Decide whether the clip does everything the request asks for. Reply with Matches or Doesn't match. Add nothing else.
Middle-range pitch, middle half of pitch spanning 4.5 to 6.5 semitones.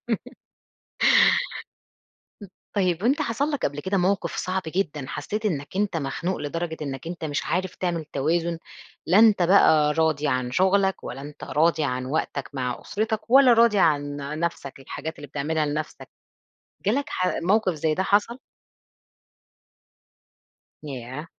Matches